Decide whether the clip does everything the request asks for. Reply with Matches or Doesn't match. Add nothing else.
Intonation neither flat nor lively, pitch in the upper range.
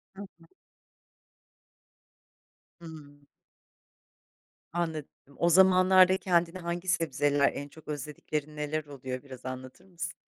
Doesn't match